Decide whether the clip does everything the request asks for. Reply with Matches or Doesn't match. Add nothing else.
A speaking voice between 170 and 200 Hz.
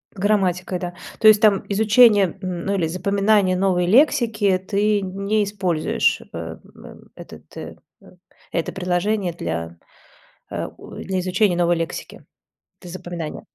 Matches